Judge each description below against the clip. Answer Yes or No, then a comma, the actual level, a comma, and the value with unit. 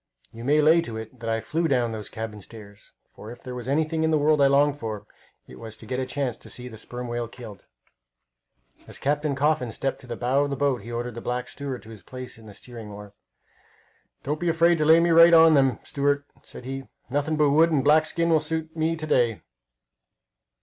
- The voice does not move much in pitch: No, average, 4.7 semitones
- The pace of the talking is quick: Yes, fast, 235 wpm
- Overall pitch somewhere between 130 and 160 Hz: Yes, low, 135 Hz